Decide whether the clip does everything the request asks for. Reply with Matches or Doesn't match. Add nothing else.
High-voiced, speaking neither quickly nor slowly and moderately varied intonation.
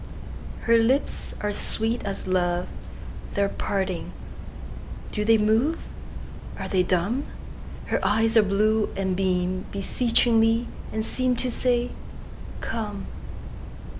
Doesn't match